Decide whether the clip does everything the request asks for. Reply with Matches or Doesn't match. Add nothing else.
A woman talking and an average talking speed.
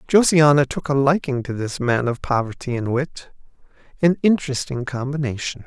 Doesn't match